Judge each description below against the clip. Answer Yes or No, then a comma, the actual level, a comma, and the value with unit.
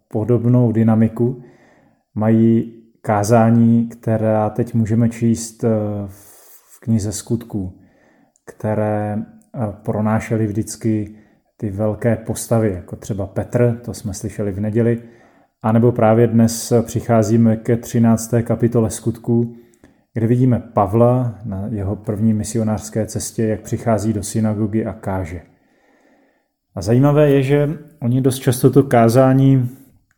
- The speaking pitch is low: Yes, low, 115 Hz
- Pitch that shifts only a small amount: Yes, narrow, 1.7 semitones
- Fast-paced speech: No, slow, 115 wpm